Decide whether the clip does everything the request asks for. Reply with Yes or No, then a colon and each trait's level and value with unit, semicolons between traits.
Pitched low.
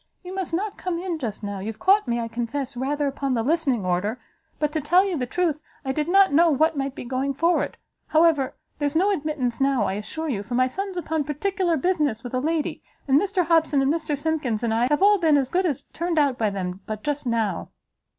No: very high, 290 Hz